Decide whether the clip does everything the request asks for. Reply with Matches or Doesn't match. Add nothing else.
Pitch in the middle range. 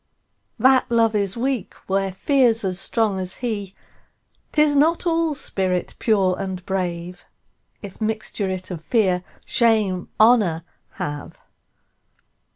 Doesn't match